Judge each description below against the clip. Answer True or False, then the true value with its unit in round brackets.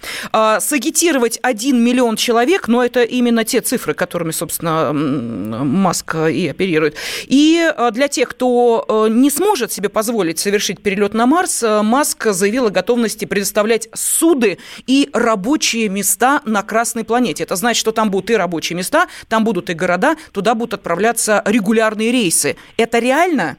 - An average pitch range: True (3.5 semitones)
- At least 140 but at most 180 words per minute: True (145 wpm)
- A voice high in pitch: True (230 Hz)